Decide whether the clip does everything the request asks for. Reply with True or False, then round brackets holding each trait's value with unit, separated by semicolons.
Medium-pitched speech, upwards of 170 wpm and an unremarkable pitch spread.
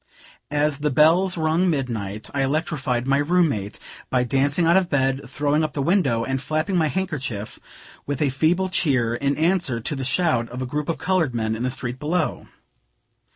True (145 Hz; 190 wpm; 4.4 semitones)